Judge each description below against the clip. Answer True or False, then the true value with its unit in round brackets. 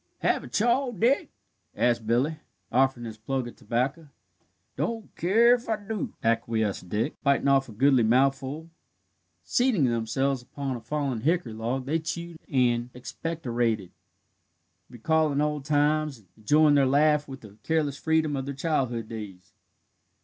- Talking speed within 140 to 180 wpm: True (145 wpm)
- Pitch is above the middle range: False (135 Hz)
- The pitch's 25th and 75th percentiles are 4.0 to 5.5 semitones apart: True (4.9 semitones)